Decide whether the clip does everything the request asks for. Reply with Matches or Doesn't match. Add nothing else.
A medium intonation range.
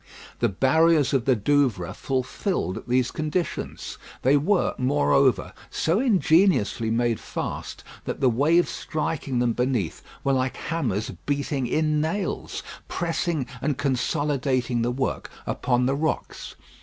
Matches